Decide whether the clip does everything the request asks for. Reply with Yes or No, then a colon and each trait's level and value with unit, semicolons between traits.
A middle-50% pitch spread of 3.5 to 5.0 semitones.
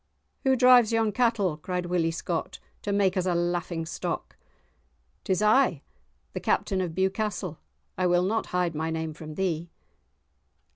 Yes: average, 3.9 semitones